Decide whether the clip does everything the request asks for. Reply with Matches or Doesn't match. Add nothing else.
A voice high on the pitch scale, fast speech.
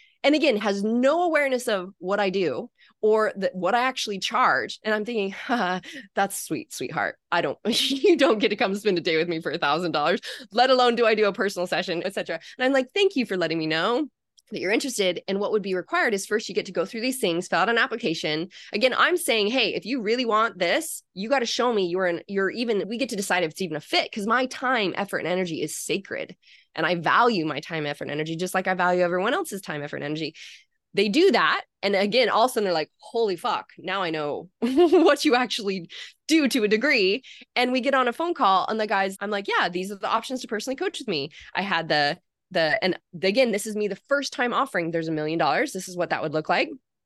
Matches